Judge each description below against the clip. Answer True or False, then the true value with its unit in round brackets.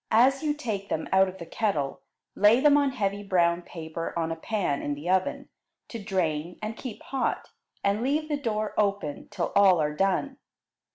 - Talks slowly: False (185 wpm)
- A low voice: False (200 Hz)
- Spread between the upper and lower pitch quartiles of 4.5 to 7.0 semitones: True (5.1 semitones)